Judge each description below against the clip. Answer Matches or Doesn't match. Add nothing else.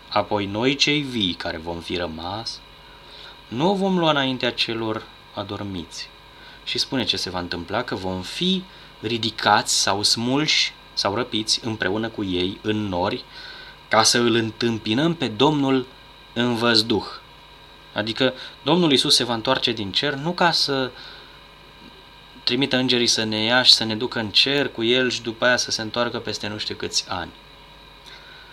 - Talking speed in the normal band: Matches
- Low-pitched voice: Matches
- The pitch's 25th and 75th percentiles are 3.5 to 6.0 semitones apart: Matches